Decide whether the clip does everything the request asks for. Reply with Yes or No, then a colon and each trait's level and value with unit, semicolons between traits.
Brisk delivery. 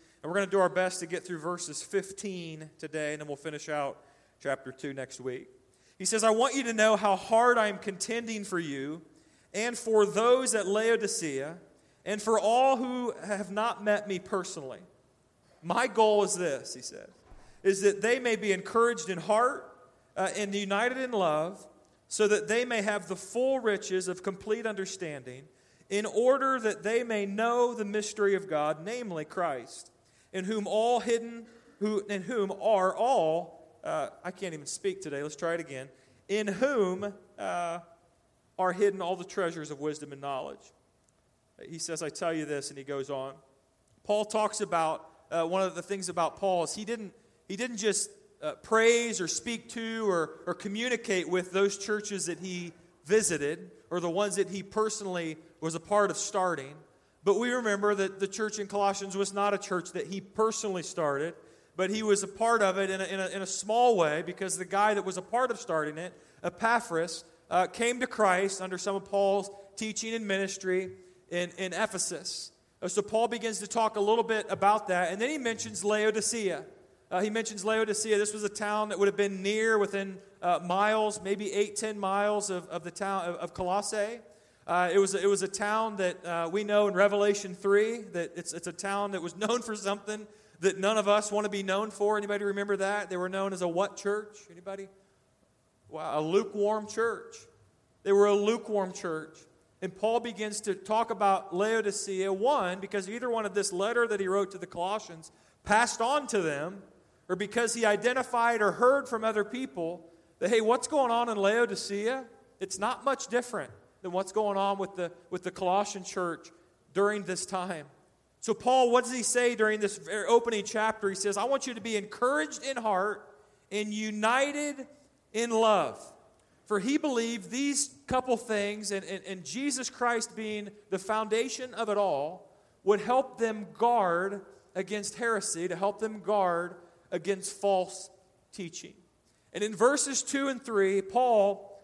No: average, 190 wpm